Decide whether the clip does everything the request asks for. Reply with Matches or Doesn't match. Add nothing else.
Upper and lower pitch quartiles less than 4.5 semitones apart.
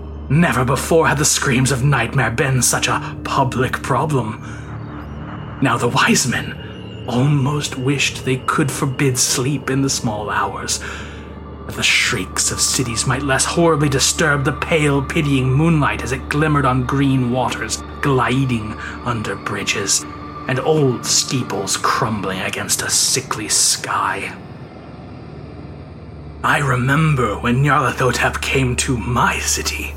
Doesn't match